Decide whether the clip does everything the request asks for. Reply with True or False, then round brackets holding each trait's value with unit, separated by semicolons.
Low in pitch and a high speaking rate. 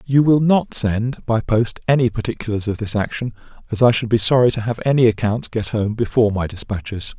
True (115 Hz; 210 wpm)